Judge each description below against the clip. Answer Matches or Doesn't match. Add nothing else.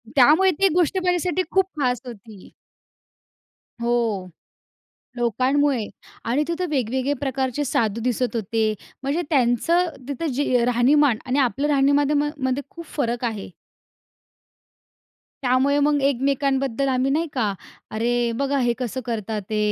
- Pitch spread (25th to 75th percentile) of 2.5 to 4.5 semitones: Matches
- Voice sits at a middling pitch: Doesn't match